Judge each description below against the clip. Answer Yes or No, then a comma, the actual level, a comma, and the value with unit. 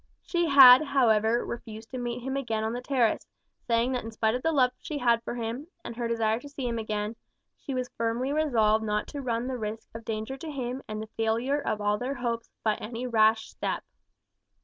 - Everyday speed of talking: No, fast, 215 wpm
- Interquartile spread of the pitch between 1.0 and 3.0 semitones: Yes, average, 2.7 semitones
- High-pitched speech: Yes, high, 235 Hz